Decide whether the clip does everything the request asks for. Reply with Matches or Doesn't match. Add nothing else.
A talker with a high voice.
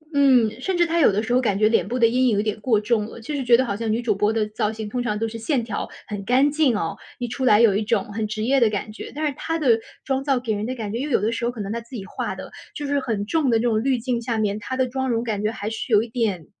Matches